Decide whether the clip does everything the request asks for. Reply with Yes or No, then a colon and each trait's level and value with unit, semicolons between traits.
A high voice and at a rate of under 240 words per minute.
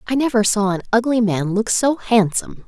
Yes: high, 220 Hz; average, 200 wpm